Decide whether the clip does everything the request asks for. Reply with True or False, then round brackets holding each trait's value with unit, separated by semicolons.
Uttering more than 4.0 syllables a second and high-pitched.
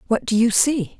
True (4.9 syllables/s; 225 Hz)